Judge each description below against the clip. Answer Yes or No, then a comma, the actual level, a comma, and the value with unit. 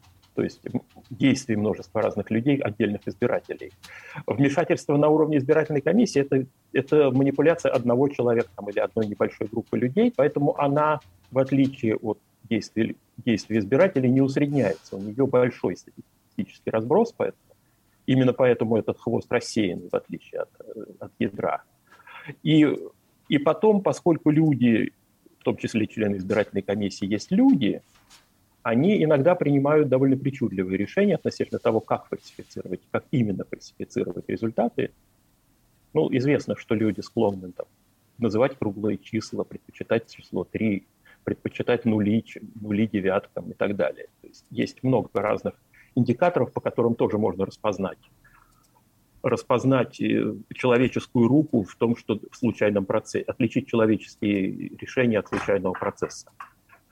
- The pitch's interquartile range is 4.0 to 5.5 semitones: Yes, average, 5.1 semitones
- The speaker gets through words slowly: No, average, 125 wpm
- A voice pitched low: Yes, low, 120 Hz